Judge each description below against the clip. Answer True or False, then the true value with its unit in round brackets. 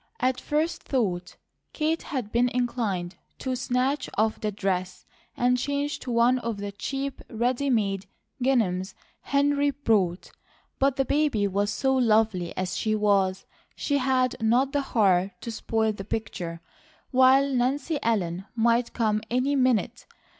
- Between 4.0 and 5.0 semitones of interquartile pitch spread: True (4.7 semitones)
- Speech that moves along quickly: False (145 wpm)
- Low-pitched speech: False (235 Hz)